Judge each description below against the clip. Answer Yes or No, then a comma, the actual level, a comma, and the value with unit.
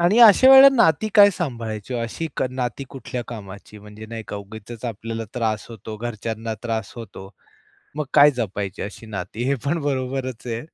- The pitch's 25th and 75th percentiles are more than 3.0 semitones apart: Yes, average, 3.9 semitones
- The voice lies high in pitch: No, low, 115 Hz